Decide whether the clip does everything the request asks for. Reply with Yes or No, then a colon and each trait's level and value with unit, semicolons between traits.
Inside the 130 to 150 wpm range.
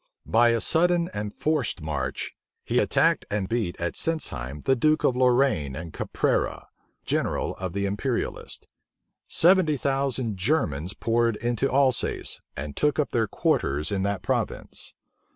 Yes: average, 140 wpm